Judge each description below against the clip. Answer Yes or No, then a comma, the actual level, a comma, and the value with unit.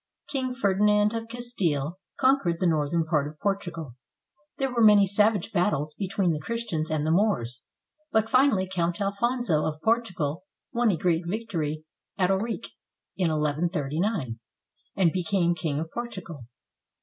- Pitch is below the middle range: No, medium, 185 Hz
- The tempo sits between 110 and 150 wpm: Yes, average, 145 wpm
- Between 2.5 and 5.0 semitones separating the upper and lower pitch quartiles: No, wide, 5.6 semitones